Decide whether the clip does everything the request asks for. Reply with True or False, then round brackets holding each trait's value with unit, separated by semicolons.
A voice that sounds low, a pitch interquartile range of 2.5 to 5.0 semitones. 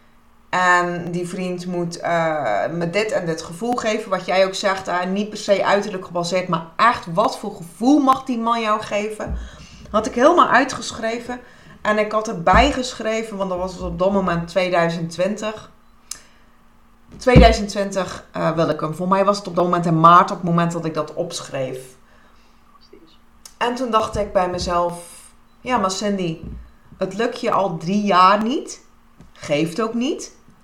False (190 Hz; 3.8 semitones)